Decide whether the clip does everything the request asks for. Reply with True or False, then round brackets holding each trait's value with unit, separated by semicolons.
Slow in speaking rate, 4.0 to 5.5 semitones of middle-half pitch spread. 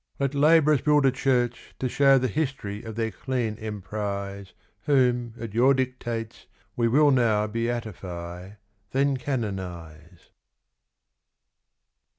True (115 wpm; 4.5 semitones)